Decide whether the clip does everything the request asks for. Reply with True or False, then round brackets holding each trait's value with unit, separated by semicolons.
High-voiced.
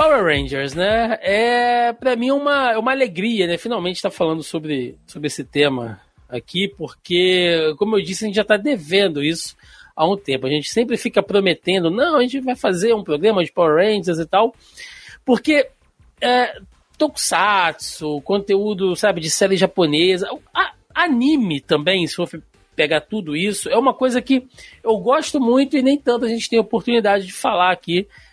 True (200 Hz)